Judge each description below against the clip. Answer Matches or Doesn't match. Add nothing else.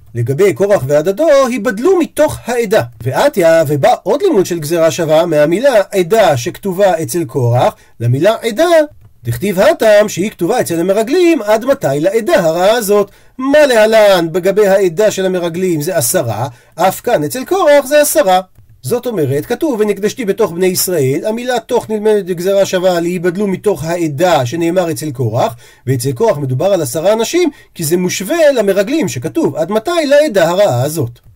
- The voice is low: Doesn't match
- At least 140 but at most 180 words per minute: Matches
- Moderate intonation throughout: Doesn't match